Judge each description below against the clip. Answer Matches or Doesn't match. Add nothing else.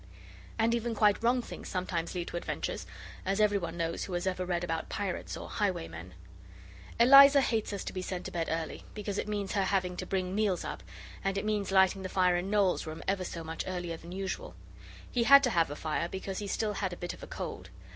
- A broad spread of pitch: Doesn't match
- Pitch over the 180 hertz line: Matches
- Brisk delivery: Matches